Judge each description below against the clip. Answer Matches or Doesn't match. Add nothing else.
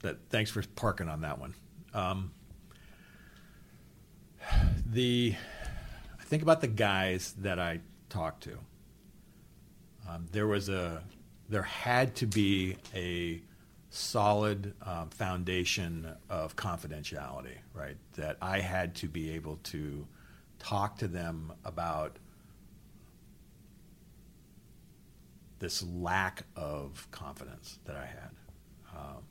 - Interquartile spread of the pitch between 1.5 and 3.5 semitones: Doesn't match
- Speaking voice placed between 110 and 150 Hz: Doesn't match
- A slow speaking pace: Matches